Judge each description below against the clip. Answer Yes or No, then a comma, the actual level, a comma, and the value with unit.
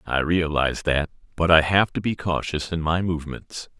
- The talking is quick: No, average, 190 wpm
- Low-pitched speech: Yes, very low, 80 Hz